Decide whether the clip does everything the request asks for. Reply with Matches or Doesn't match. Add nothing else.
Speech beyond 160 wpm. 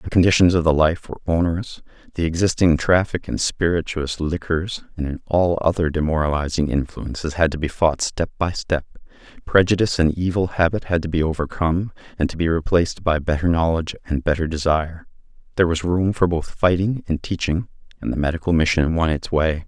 Matches